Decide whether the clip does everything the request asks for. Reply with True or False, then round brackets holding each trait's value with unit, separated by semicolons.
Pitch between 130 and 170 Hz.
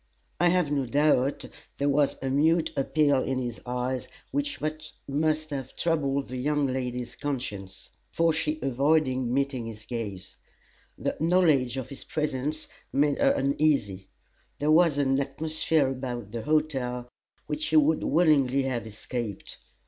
True (140 Hz)